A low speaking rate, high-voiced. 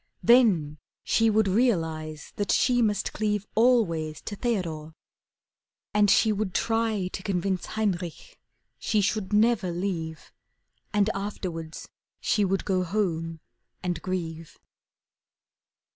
Yes: slow, 115 wpm; high, 195 Hz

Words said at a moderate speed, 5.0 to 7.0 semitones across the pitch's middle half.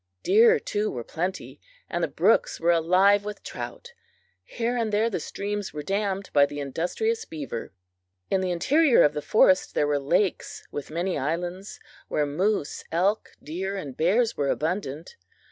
Yes: average, 160 wpm; average, 5.3 semitones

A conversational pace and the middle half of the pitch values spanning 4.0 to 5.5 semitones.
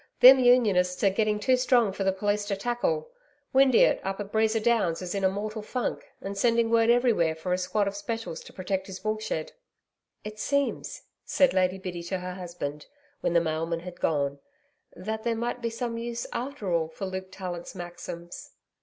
Yes: average, 190 wpm; average, 4.3 semitones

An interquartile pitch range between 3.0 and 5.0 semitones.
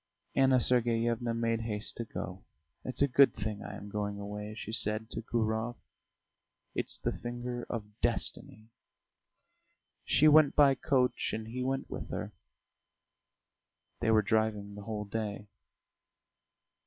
No: narrow, 2.6 semitones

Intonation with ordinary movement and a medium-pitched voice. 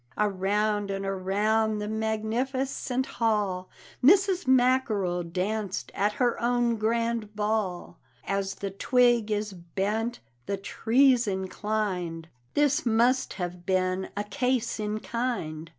No: average, 3.6 semitones; high, 215 Hz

